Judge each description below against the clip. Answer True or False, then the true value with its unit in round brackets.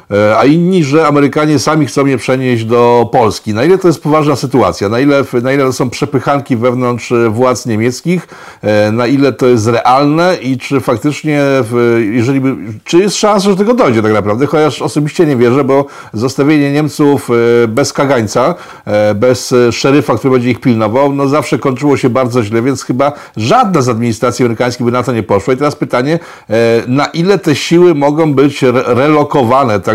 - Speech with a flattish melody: False (3.6 semitones)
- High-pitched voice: False (135 Hz)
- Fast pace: True (170 wpm)